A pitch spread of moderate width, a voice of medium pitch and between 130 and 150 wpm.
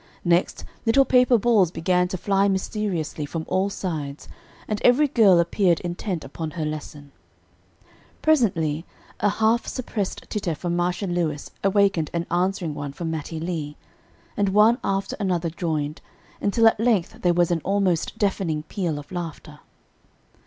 Yes: average, 4.0 semitones; medium, 180 Hz; average, 145 wpm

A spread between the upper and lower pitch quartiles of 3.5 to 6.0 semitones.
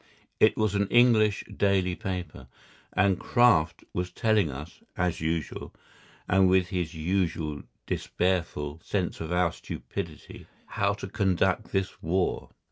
No: average, 3.0 semitones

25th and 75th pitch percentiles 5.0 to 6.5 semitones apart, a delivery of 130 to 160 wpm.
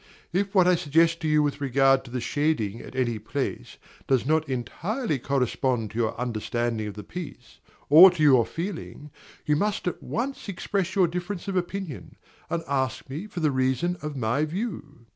No: wide, 5.6 semitones; average, 180 wpm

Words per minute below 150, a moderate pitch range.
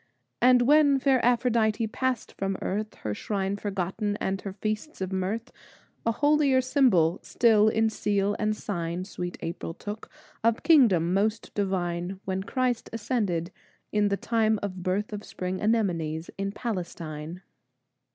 Yes: average, 140 wpm; average, 3.8 semitones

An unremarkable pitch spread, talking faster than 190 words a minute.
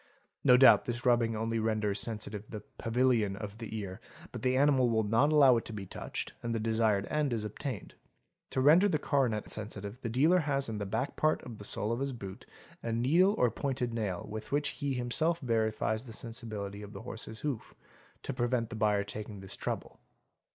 Yes: average, 3.5 semitones; fast, 205 wpm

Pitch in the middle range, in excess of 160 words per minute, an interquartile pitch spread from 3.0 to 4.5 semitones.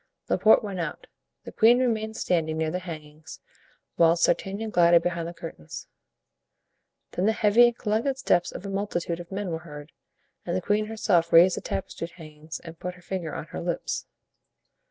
Yes: medium, 175 Hz; average, 175 wpm; average, 3.9 semitones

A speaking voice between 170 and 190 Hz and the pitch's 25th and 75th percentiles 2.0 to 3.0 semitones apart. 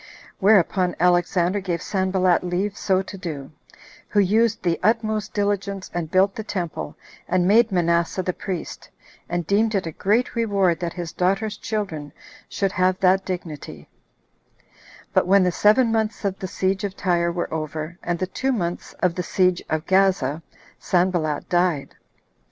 Yes: medium, 185 Hz; narrow, 2.5 semitones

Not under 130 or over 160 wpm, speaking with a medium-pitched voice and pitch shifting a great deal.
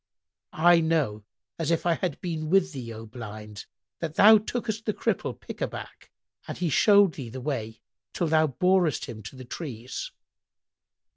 No: average, 170 wpm; medium, 155 Hz; wide, 7.1 semitones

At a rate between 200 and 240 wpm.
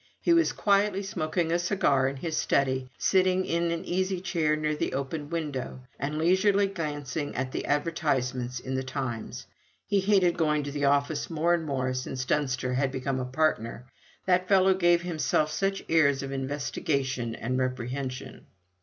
No: average, 170 wpm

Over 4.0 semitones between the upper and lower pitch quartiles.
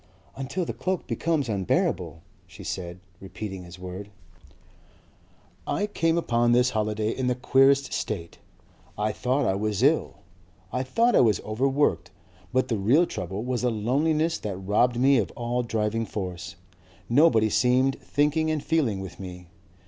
Yes: average, 5.1 semitones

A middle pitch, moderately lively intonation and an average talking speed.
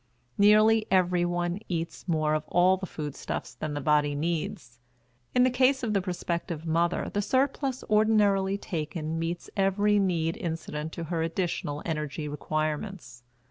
Yes: medium, 175 Hz; average, 4.4 semitones; average, 145 wpm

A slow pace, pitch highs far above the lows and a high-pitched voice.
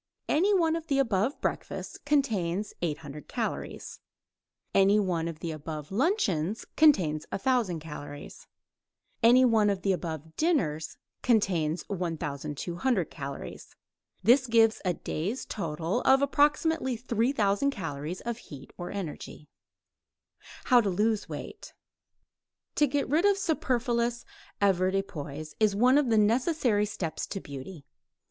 Yes: slow, 125 wpm; wide, 7.6 semitones; high, 205 Hz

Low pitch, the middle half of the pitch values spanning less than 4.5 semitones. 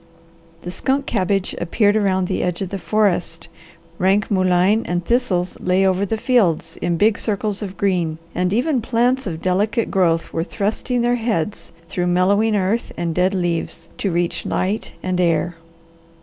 No: high, 190 Hz; average, 3.4 semitones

